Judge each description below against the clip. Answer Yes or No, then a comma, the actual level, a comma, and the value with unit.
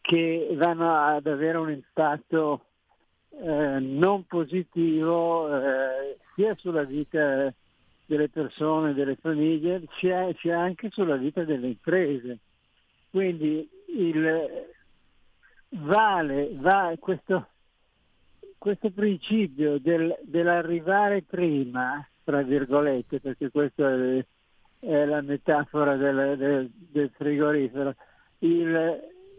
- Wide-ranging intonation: No, average, 3.6 semitones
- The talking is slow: Yes, slow, 100 wpm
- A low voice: No, medium, 155 Hz